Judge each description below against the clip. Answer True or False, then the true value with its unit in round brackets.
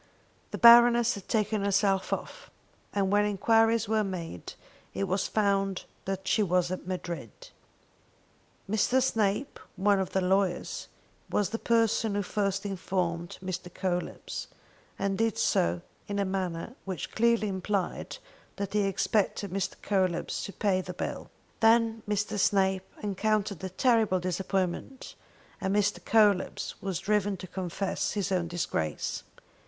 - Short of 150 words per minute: True (135 wpm)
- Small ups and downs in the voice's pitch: True (2.3 semitones)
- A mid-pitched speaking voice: False (195 Hz)